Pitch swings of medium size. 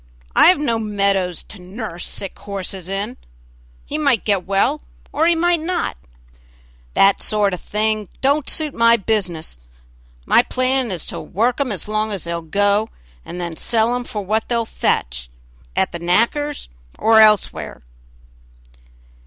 Yes: average, 4.6 semitones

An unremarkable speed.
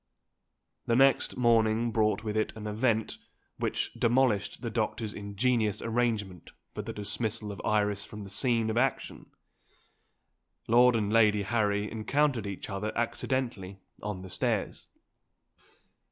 No: slow, 130 wpm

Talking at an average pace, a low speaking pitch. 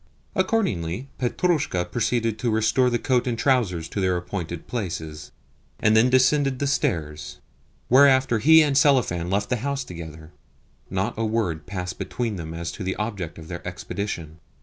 Yes: average, 160 wpm; low, 110 Hz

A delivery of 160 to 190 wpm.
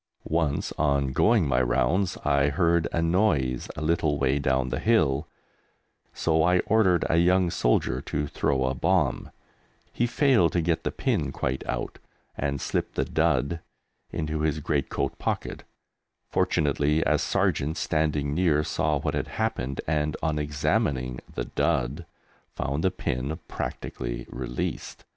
No: average, 145 wpm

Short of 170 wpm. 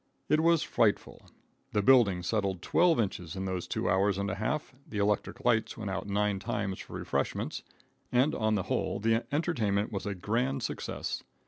No: average, 180 wpm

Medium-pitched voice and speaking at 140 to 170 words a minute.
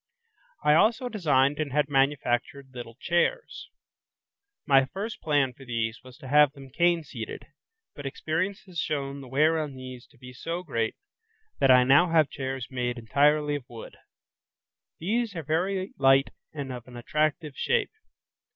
Yes: medium, 145 Hz; average, 160 wpm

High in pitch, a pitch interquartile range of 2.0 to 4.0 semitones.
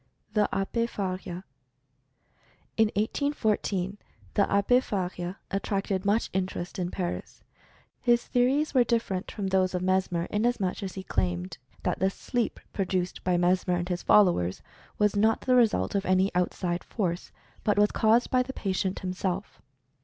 Yes: high, 195 Hz; average, 3.1 semitones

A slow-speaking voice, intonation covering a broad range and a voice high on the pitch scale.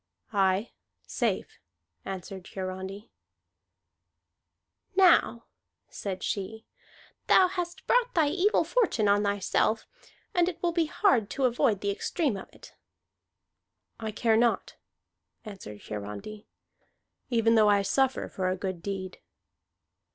Yes: slow, 115 wpm; wide, 7.0 semitones; high, 215 Hz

